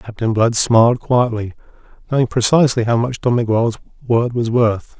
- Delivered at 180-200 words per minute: No, average, 155 wpm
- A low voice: Yes, low, 115 Hz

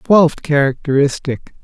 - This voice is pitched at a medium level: Yes, medium, 150 Hz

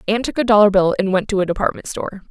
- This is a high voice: Yes, high, 200 Hz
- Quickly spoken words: Yes, fast, 285 wpm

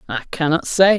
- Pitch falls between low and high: Yes, medium, 160 Hz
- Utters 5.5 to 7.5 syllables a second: No, 5.2 syllables/s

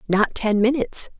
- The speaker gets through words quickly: No, average, 150 wpm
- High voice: Yes, high, 225 Hz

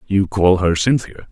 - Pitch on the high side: No, very low, 95 Hz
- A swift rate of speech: No, average, 180 wpm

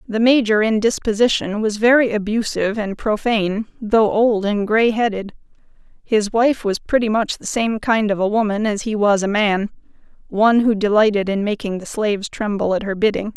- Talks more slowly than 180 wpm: No, average, 185 wpm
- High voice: Yes, high, 215 Hz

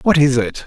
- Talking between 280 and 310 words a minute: No, fast, 270 wpm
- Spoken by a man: Yes, male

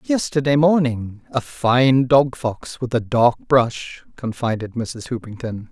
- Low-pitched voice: Yes, low, 125 Hz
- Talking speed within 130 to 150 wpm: Yes, slow, 135 wpm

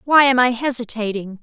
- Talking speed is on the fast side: No, average, 170 wpm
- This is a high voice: Yes, high, 240 Hz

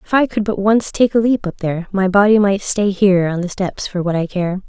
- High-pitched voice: Yes, high, 195 Hz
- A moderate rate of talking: No, fast, 280 wpm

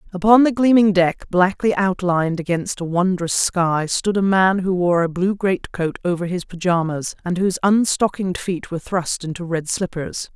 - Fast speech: No, average, 175 wpm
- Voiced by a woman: Yes, female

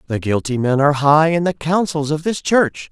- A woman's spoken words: No, male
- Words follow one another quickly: Yes, fast, 225 wpm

